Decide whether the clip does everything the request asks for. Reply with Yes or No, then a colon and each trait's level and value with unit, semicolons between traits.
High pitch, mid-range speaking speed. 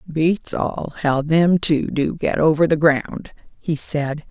No: medium, 155 Hz; average, 165 wpm